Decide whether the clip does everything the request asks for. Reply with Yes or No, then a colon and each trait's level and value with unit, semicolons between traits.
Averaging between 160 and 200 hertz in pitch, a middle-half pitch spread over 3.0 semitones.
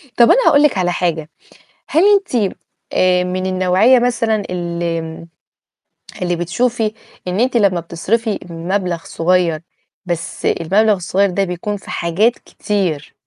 Yes: medium, 185 Hz; average, 4.1 semitones